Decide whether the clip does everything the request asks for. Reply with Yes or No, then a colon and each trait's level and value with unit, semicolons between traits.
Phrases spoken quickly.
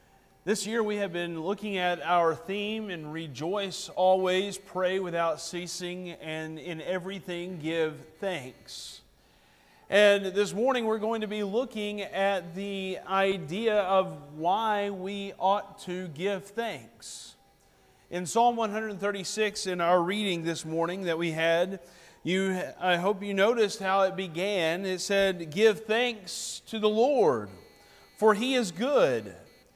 No: slow, 135 wpm